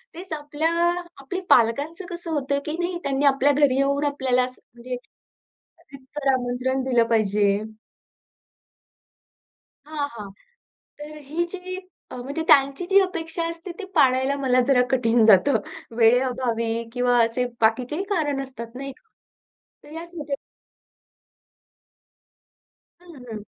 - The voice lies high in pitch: Yes, very high, 275 Hz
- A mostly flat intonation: No, average, 3.7 semitones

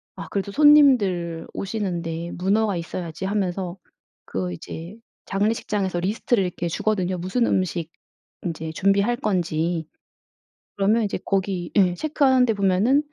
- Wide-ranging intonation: No, average, 3.6 semitones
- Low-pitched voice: No, high, 190 Hz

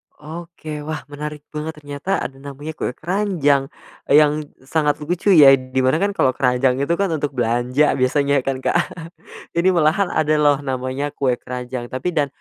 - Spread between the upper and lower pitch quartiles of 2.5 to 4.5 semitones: Yes, average, 3.1 semitones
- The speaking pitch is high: No, medium, 145 Hz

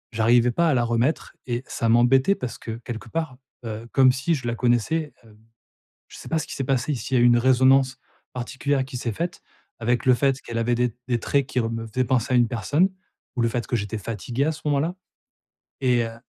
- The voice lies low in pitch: Yes, low, 125 Hz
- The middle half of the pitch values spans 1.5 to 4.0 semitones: Yes, narrow, 2.6 semitones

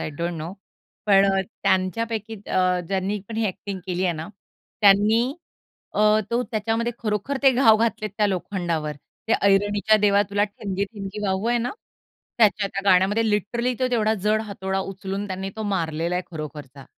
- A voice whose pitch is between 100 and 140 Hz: No, high, 200 Hz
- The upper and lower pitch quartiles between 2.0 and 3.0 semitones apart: Yes, narrow, 2.6 semitones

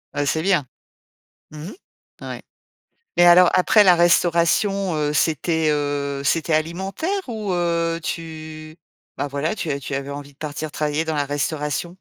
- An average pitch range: Yes, average, 3.0 semitones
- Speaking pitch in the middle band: Yes, medium, 160 Hz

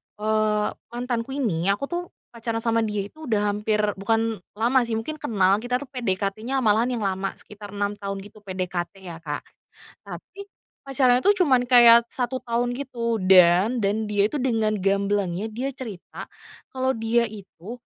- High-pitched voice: Yes, high, 220 Hz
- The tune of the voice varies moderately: Yes, average, 3.5 semitones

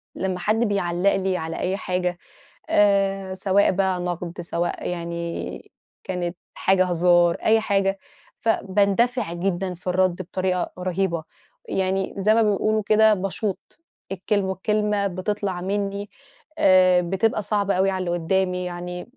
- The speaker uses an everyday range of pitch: No, narrow, 2.0 semitones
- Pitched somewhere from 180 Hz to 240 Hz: Yes, high, 190 Hz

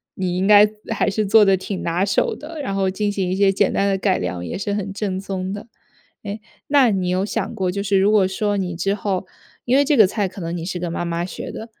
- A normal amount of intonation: No, narrow, 2.0 semitones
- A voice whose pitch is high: Yes, high, 195 Hz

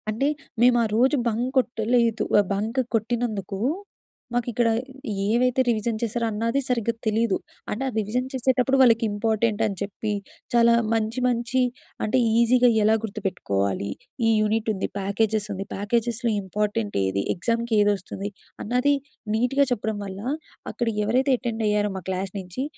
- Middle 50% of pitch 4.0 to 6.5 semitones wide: No, average, 2.7 semitones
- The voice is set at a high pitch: Yes, high, 225 Hz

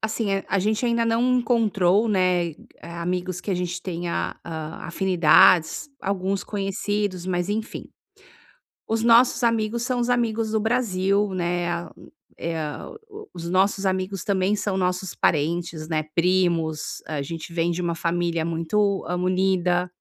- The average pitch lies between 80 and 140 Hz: No, medium, 185 Hz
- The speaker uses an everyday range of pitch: Yes, average, 3.6 semitones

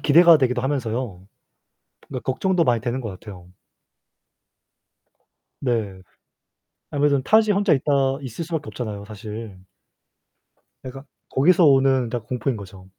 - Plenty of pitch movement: No, average, 4.6 semitones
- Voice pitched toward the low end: Yes, low, 130 Hz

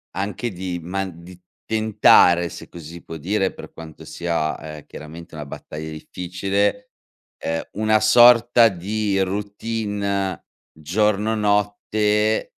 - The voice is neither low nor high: No, low, 100 Hz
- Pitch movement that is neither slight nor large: Yes, average, 3.8 semitones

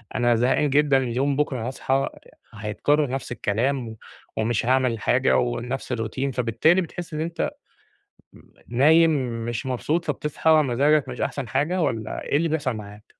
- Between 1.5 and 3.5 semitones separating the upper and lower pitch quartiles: No, average, 3.9 semitones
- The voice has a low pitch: Yes, low, 130 Hz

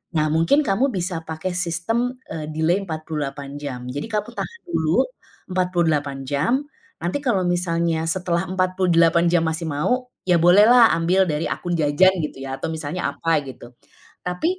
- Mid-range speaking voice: Yes, medium, 170 Hz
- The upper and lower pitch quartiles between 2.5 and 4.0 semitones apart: Yes, average, 2.9 semitones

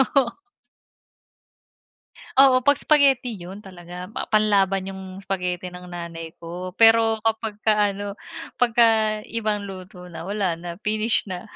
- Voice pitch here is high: Yes, high, 200 Hz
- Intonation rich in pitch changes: No, average, 3.8 semitones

